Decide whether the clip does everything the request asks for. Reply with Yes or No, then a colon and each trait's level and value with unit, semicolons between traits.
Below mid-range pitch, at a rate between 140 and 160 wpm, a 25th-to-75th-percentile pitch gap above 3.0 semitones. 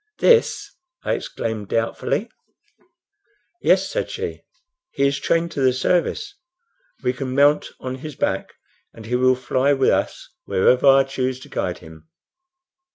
No: low, 130 Hz; average, 145 wpm; narrow, 2.4 semitones